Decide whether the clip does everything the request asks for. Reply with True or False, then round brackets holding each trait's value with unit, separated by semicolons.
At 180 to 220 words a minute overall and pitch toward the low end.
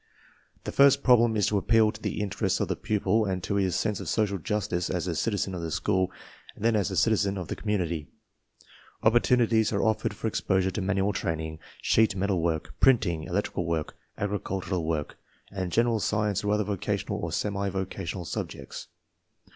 True (190 wpm; 100 Hz)